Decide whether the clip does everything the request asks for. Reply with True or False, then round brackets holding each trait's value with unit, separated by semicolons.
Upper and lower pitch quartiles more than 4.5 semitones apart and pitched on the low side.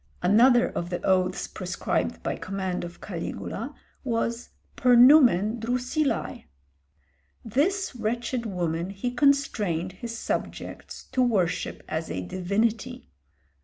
False (5.2 semitones; 225 Hz)